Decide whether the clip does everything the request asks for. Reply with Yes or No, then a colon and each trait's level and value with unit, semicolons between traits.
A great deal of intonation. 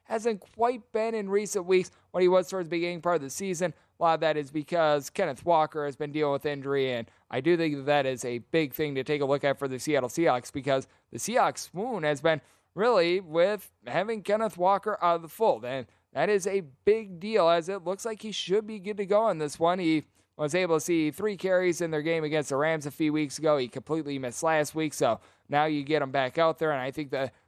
No: average, 4.3 semitones